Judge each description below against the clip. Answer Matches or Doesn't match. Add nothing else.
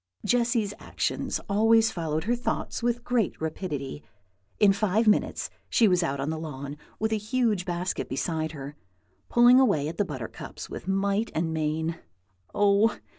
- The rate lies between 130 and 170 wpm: Matches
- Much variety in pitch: Matches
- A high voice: Matches